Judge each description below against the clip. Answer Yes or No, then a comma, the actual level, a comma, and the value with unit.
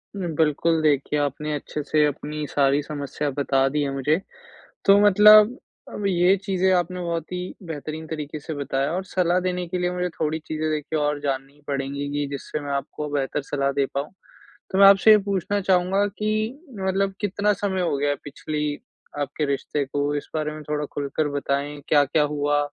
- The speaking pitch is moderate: Yes, medium, 150 Hz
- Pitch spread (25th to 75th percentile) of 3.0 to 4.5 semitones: Yes, average, 4.1 semitones